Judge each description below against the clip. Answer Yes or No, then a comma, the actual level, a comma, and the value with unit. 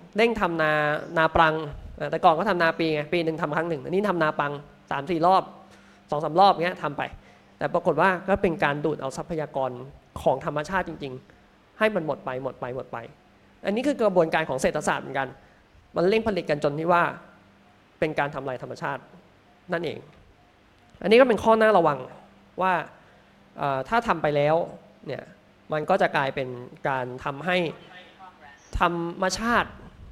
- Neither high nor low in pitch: Yes, medium, 160 Hz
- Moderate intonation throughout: Yes, average, 3.9 semitones